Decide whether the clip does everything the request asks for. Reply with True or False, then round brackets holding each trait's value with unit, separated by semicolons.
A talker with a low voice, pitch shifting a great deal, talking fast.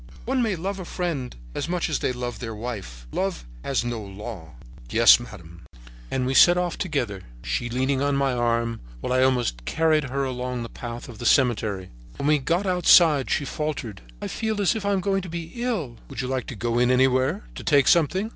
True (130 Hz; 6.1 semitones; 210 wpm)